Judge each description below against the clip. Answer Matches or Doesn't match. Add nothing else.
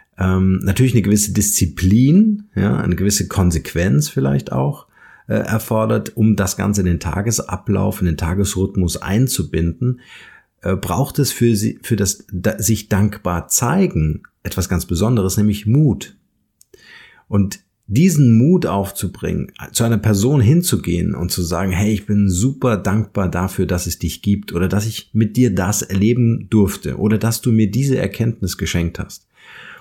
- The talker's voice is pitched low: Matches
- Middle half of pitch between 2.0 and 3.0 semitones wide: Doesn't match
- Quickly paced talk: Doesn't match